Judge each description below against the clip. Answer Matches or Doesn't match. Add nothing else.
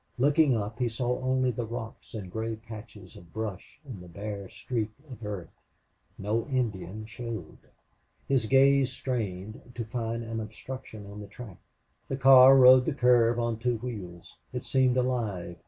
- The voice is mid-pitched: Doesn't match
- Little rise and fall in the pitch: Doesn't match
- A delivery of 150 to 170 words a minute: Matches